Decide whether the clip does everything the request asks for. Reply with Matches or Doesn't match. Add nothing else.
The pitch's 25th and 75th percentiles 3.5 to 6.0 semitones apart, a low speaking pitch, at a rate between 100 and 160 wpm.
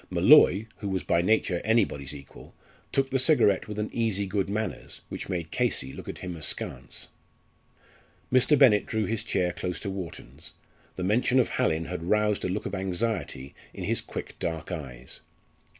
Doesn't match